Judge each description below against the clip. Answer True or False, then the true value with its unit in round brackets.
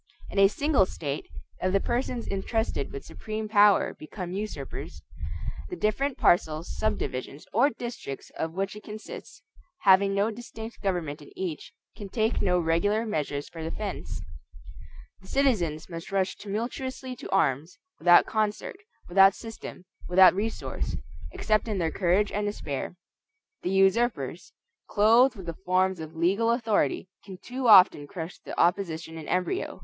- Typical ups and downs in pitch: True (4.5 semitones)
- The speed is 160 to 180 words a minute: False (145 wpm)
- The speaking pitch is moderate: False (195 Hz)